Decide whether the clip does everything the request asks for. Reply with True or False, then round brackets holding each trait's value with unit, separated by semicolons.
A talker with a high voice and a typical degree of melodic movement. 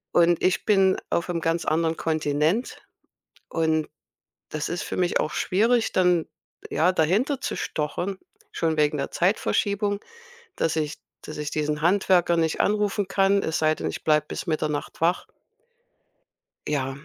False (165 Hz; 3.7 semitones)